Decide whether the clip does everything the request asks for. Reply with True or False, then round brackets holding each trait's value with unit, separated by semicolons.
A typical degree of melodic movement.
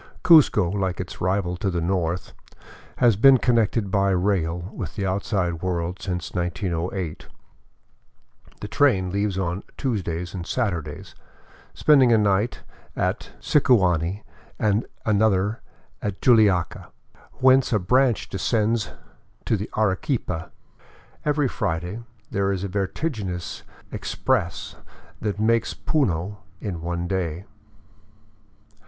True (3.7 semitones)